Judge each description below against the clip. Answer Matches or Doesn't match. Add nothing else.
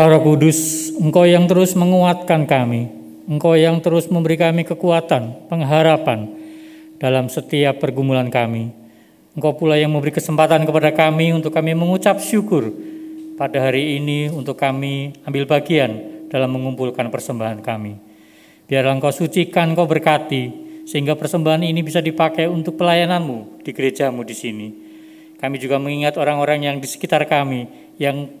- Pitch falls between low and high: Matches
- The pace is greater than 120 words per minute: Matches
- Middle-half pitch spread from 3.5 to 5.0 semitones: Matches